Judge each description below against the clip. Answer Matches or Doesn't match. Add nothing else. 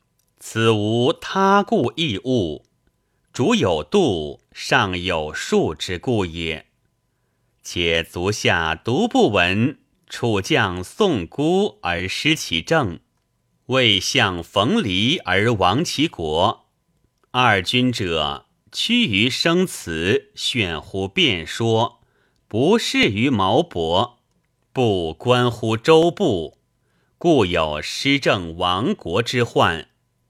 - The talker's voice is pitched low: Matches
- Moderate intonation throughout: Doesn't match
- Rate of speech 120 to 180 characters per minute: Matches